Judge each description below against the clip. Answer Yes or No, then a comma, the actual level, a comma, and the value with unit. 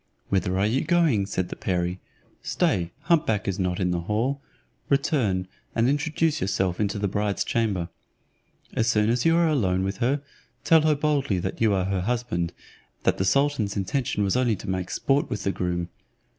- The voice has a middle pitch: No, low, 105 Hz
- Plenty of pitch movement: Yes, wide, 6.7 semitones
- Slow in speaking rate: No, average, 185 wpm